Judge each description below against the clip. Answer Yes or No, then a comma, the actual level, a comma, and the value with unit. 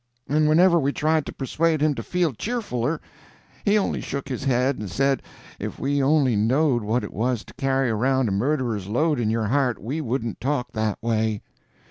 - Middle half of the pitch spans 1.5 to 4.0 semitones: No, average, 4.7 semitones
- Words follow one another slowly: No, average, 190 wpm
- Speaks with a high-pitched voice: No, low, 135 Hz